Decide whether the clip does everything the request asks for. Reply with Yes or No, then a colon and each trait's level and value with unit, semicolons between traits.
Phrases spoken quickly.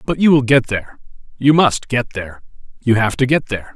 Yes: fast, 225 wpm